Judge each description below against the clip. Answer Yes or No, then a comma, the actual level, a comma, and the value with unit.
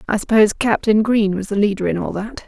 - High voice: Yes, high, 210 Hz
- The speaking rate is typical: No, fast, 245 wpm